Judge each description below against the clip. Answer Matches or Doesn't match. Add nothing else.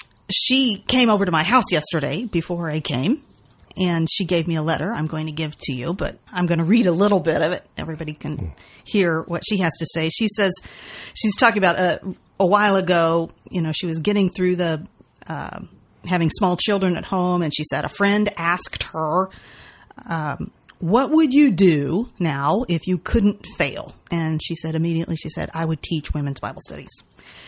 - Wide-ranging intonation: Doesn't match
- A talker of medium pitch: Matches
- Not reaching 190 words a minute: Doesn't match